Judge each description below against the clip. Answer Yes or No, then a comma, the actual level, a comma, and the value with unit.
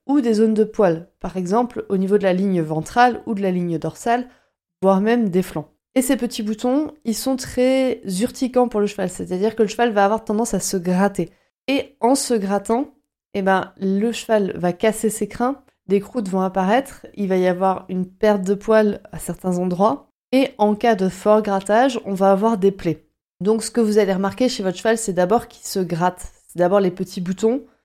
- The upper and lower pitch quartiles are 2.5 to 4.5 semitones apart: Yes, average, 3.7 semitones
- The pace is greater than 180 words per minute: Yes, average, 215 wpm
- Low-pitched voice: No, high, 210 Hz